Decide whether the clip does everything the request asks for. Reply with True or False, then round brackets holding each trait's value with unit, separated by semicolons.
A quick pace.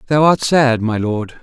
True (210 wpm)